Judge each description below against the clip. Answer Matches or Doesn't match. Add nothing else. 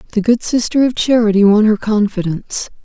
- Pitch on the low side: Doesn't match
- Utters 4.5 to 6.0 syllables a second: Matches